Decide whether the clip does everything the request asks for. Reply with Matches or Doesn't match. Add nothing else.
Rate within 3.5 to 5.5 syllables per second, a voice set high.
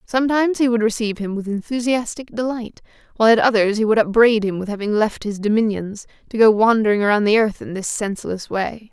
Doesn't match